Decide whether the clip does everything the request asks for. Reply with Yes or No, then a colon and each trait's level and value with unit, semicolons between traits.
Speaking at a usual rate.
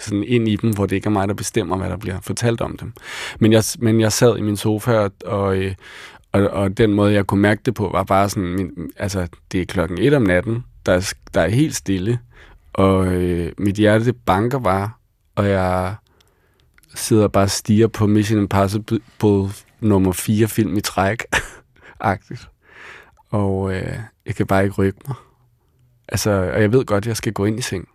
Yes: average, 200 wpm